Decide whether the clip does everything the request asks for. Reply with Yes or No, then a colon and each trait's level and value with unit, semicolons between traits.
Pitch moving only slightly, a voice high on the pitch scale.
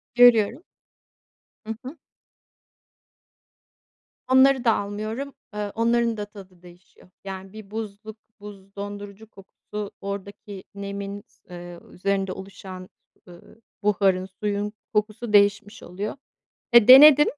Yes: narrow, 2.2 semitones; high, 205 Hz